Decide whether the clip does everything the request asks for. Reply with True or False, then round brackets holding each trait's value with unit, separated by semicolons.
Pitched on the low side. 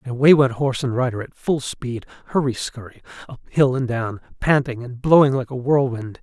True (130 Hz)